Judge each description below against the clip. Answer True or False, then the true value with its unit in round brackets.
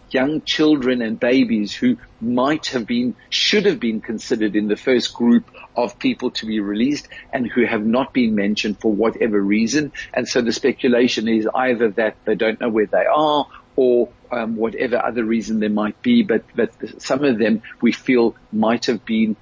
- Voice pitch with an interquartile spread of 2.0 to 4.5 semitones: True (3.0 semitones)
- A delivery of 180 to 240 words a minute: True (190 wpm)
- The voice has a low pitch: True (120 Hz)